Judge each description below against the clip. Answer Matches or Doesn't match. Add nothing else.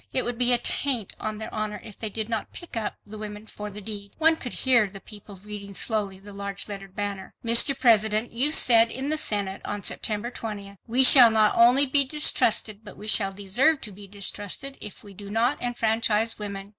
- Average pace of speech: Doesn't match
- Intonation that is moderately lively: Matches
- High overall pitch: Matches